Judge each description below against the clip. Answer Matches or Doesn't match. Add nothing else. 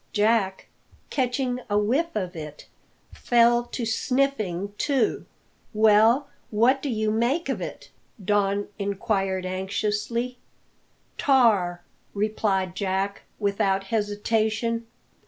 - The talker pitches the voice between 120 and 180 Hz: Doesn't match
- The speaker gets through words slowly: Matches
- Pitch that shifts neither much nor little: Matches